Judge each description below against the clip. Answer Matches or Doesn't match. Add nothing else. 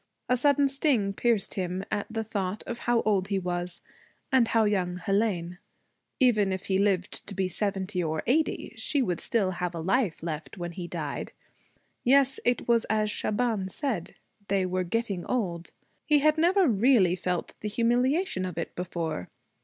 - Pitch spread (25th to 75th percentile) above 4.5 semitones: Matches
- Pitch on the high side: Matches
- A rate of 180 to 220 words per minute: Doesn't match